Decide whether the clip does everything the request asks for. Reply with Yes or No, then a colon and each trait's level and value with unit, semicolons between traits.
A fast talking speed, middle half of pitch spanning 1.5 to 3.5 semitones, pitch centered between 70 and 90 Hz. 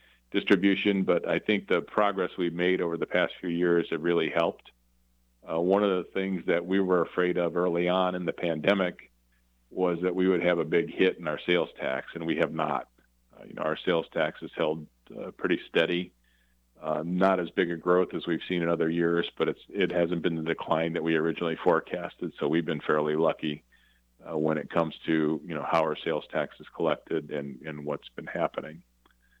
Yes: fast, 210 wpm; average, 2.9 semitones; very low, 85 Hz